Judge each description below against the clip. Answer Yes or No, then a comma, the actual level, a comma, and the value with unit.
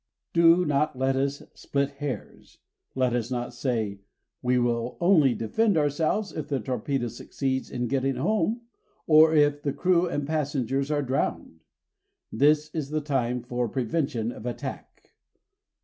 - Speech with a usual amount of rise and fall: Yes, average, 3.7 semitones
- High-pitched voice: No, medium, 140 Hz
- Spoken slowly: No, average, 150 wpm